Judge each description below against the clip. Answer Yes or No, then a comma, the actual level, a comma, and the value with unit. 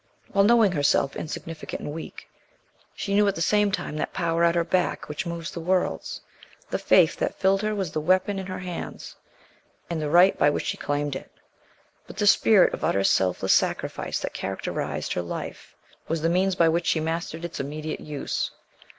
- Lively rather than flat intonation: No, average, 3.7 semitones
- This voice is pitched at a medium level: Yes, medium, 170 Hz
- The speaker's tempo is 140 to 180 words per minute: No, average, 195 wpm